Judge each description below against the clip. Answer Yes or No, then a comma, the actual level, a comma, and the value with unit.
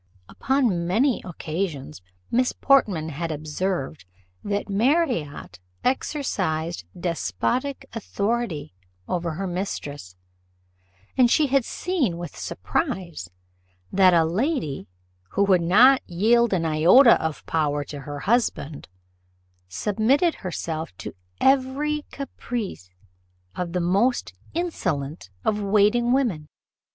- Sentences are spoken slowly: Yes, slow, 105 wpm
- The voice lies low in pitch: No, high, 190 Hz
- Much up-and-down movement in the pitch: Yes, wide, 7.7 semitones